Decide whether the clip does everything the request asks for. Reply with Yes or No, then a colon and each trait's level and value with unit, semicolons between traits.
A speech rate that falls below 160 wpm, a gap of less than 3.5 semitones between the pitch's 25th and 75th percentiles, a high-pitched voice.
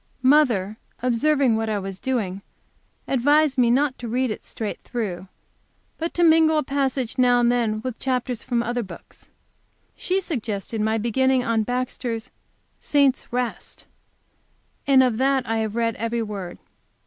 Yes: average, 150 wpm; average, 3.0 semitones; high, 245 Hz